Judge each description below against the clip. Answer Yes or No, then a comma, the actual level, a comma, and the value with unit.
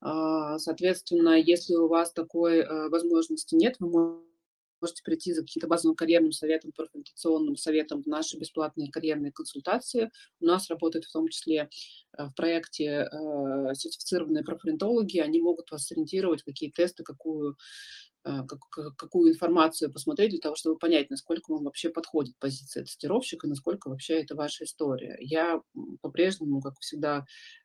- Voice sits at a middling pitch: Yes, medium, 160 Hz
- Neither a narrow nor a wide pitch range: No, narrow, 1.9 semitones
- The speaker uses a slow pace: No, average, 135 wpm